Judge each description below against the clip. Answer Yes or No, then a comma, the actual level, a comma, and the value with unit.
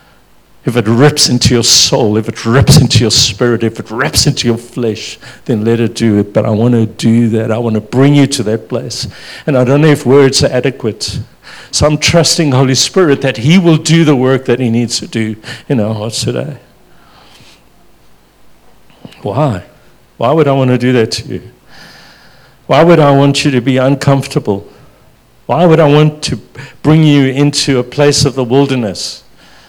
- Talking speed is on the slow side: No, average, 195 wpm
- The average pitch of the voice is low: Yes, low, 125 Hz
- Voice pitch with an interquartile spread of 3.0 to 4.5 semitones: Yes, average, 3.8 semitones